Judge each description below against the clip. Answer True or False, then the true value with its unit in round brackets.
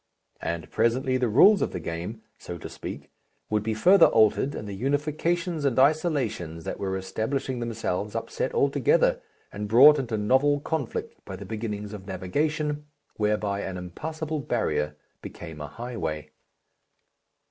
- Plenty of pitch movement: True (6.8 semitones)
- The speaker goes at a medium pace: True (145 wpm)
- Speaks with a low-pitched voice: True (115 Hz)